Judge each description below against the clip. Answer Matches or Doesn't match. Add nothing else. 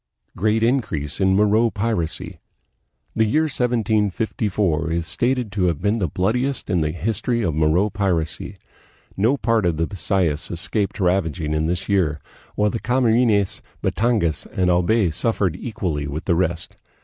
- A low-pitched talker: Matches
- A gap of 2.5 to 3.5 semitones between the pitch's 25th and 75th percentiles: Doesn't match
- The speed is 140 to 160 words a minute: Matches